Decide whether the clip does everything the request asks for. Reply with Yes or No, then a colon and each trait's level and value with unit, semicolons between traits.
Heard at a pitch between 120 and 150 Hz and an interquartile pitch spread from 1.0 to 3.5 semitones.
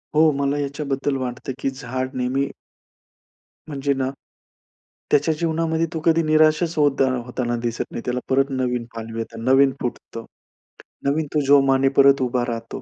Yes: low, 135 Hz; average, 2.7 semitones